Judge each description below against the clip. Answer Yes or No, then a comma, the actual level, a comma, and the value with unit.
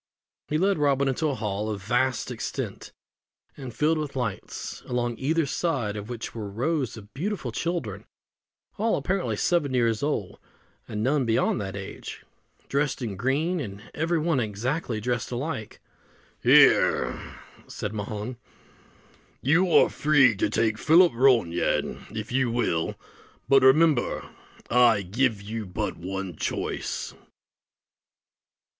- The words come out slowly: Yes, slow, 130 wpm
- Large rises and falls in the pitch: Yes, wide, 5.7 semitones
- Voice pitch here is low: Yes, low, 125 Hz